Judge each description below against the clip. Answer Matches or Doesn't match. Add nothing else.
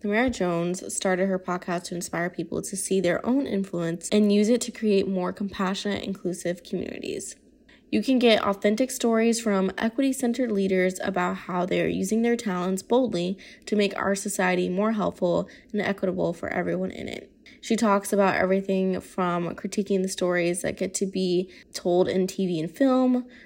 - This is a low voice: Doesn't match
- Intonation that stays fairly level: Doesn't match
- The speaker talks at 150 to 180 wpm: Matches